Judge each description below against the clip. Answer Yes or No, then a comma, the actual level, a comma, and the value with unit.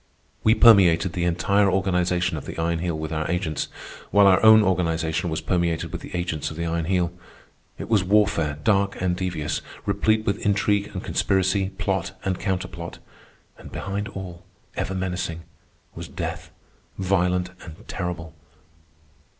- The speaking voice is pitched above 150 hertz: No, very low, 90 Hz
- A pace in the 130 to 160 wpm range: Yes, average, 150 wpm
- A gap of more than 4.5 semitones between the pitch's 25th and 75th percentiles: No, narrow, 2.6 semitones